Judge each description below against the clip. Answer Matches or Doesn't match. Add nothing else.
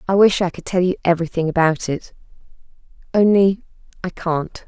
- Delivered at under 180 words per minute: Matches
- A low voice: Doesn't match